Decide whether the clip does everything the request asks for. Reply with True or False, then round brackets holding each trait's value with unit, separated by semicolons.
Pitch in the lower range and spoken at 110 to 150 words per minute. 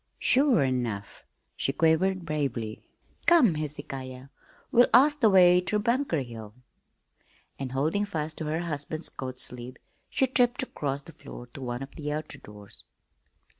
False (150 Hz; 145 wpm)